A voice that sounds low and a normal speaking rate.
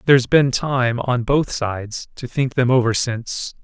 Yes: low, 125 Hz; average, 180 wpm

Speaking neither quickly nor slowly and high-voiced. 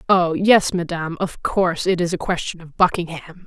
No: average, 190 wpm; medium, 175 Hz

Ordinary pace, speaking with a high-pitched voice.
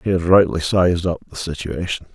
No: average, 195 wpm; very low, 85 Hz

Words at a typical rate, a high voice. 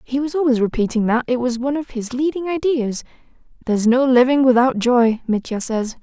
Yes: average, 190 wpm; very high, 250 Hz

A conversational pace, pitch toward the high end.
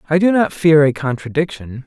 No: average, 195 wpm; medium, 150 Hz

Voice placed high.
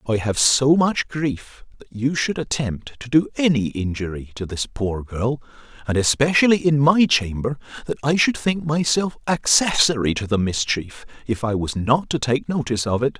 No: low, 130 Hz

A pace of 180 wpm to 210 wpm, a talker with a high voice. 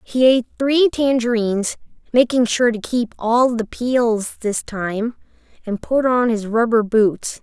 No: average, 155 wpm; high, 235 Hz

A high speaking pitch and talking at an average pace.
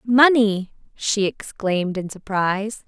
No: high, 205 Hz; slow, 105 wpm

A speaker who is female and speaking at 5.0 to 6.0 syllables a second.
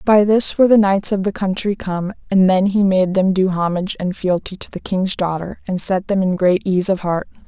Yes: female; 5.2 syllables/s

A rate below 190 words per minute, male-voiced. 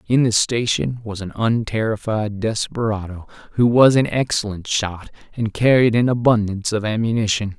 Yes: average, 140 wpm; male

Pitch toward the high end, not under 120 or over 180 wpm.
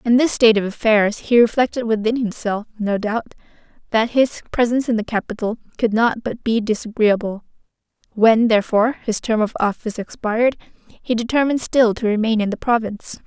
Yes: high, 225 Hz; average, 165 wpm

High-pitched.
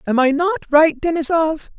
Yes: very high, 315 Hz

